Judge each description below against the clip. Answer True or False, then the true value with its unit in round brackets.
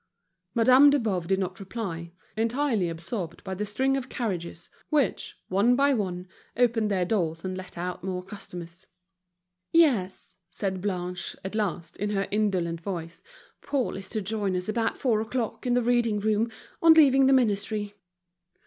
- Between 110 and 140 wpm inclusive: False (160 wpm)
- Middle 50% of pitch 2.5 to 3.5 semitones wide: False (4.6 semitones)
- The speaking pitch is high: True (205 Hz)